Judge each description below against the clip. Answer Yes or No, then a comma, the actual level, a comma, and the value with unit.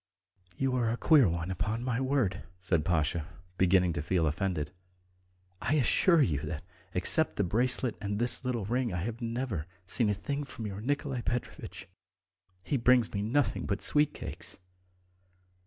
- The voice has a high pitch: No, low, 110 Hz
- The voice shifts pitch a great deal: Yes, wide, 5.9 semitones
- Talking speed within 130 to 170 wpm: Yes, average, 155 wpm